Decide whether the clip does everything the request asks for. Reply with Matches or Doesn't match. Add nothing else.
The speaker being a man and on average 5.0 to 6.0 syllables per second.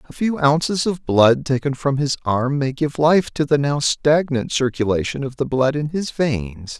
Doesn't match